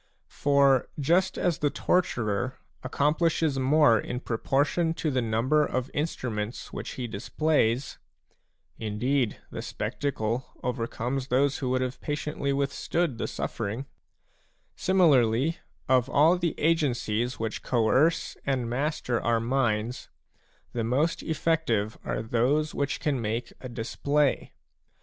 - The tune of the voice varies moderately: Yes, average, 4.2 semitones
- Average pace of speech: No, slow, 125 wpm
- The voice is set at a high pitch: No, low, 130 Hz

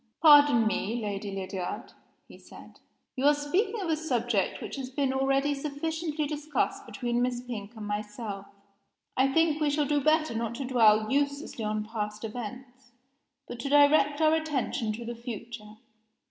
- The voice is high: Yes, very high, 255 Hz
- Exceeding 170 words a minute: No, average, 160 wpm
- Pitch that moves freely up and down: No, average, 4.9 semitones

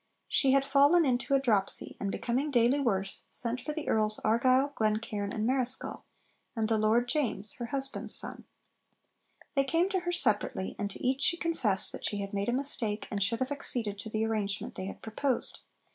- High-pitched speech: Yes, high, 240 Hz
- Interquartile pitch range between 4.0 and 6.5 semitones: Yes, average, 4.4 semitones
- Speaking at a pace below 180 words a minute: No, average, 190 wpm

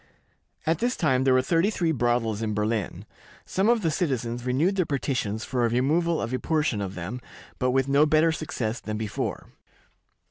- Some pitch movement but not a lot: No, wide, 5.7 semitones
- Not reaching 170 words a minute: No, average, 185 wpm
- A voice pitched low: Yes, low, 130 Hz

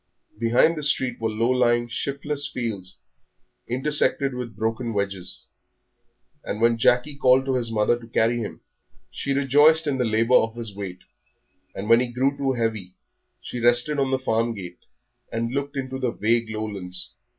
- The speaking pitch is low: Yes, low, 120 Hz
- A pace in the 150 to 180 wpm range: Yes, average, 165 wpm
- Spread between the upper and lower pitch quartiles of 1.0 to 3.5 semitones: Yes, average, 3.1 semitones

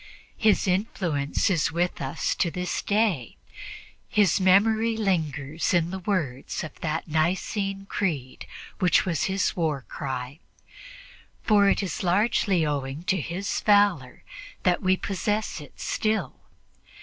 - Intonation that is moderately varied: Yes, average, 4.6 semitones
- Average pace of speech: No, slow, 125 wpm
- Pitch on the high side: No, medium, 180 Hz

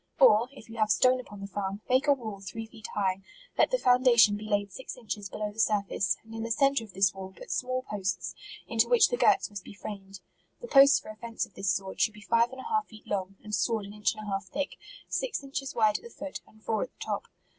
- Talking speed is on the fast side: Yes, fast, 265 wpm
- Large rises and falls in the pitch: No, average, 4.1 semitones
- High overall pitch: Yes, high, 215 Hz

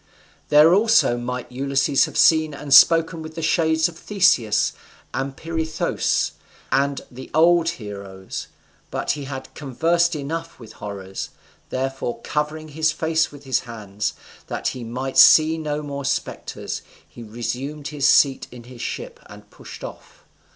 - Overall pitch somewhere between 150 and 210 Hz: No, medium, 140 Hz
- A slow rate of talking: No, average, 145 wpm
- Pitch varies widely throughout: No, average, 4.1 semitones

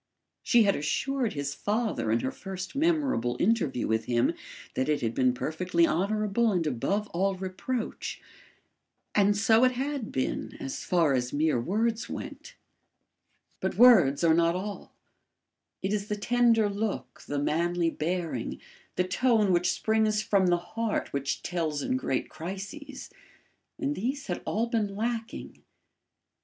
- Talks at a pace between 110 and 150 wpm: Yes, average, 145 wpm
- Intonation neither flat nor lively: No, wide, 6.1 semitones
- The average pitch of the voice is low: No, high, 195 Hz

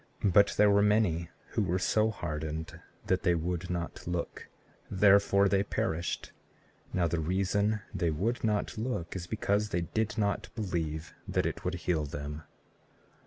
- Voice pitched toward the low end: Yes, very low, 90 Hz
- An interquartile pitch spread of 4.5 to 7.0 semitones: No, average, 3.4 semitones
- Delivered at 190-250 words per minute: No, average, 155 wpm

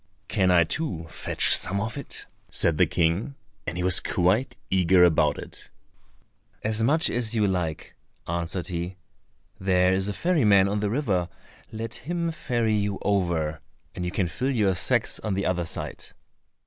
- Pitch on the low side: Yes, very low, 95 Hz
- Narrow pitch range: No, average, 4.2 semitones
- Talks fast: No, average, 170 wpm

